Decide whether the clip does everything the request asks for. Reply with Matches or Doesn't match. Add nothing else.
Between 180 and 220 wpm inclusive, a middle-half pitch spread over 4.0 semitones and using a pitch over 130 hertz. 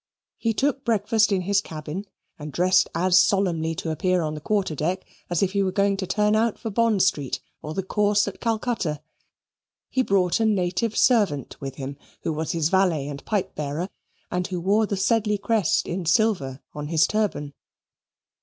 Matches